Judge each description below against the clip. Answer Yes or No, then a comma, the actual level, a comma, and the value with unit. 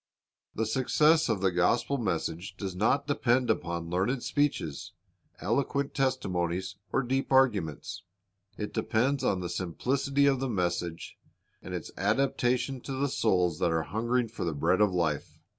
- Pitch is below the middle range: Yes, low, 110 Hz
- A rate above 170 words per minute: No, average, 155 wpm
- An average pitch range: No, wide, 6.9 semitones